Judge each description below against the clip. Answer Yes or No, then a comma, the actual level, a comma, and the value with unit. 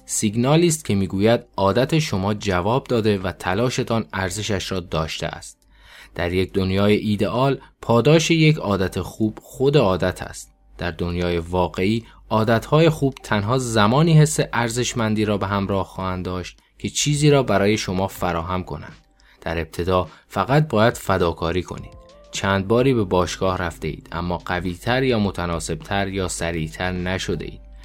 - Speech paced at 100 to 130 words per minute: No, average, 140 wpm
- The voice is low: Yes, low, 100 Hz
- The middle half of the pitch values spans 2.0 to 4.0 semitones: No, average, 4.7 semitones